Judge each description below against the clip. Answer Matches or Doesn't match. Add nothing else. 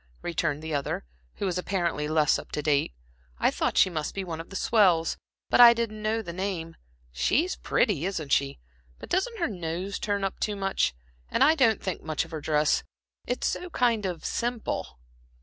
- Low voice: Doesn't match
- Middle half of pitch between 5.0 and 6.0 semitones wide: Matches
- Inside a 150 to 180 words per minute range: Doesn't match